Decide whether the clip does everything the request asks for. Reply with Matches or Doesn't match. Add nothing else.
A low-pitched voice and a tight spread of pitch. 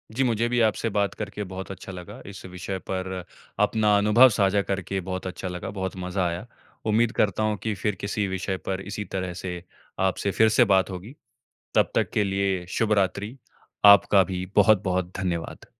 Matches